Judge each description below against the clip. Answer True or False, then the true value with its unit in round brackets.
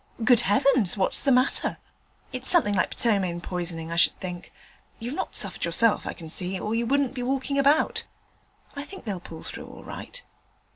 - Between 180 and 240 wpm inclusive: True (185 wpm)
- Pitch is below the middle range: False (225 Hz)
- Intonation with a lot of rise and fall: True (6.6 semitones)